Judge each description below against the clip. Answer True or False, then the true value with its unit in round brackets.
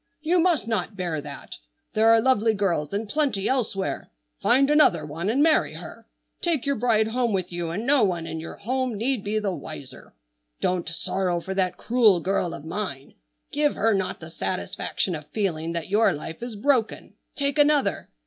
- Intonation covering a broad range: True (6.4 semitones)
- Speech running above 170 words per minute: True (185 wpm)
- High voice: True (205 Hz)